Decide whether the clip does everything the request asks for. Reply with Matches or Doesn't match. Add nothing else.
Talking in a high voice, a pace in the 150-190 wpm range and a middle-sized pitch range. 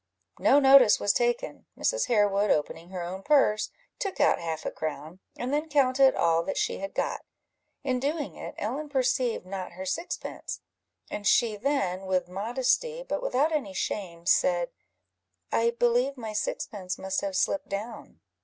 Doesn't match